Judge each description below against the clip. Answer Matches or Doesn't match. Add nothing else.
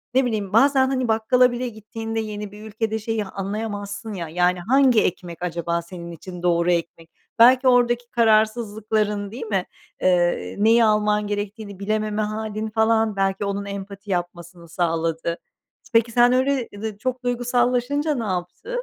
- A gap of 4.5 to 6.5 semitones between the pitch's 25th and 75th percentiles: Doesn't match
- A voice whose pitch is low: Doesn't match